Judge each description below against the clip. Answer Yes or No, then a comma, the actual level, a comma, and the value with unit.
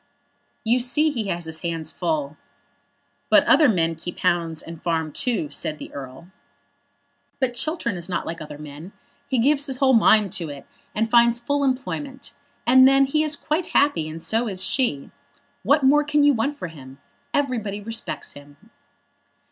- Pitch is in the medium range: No, high, 220 Hz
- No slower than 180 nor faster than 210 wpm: No, average, 170 wpm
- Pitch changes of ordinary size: No, wide, 8.6 semitones